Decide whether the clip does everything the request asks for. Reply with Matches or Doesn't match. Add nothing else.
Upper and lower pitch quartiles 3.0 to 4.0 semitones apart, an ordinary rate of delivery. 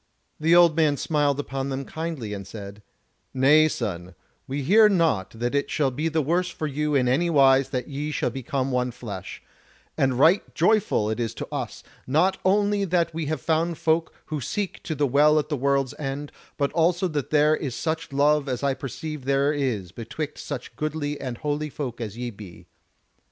Matches